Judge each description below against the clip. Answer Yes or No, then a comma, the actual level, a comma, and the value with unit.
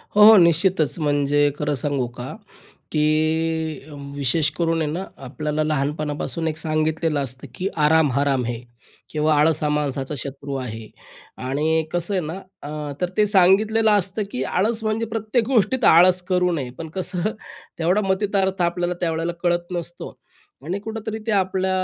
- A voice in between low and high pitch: Yes, medium, 160 Hz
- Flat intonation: No, average, 4.0 semitones